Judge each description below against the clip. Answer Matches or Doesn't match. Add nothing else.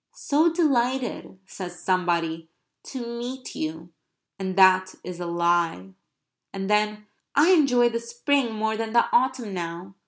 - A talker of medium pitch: Doesn't match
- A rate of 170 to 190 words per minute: Doesn't match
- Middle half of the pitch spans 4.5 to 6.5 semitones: Matches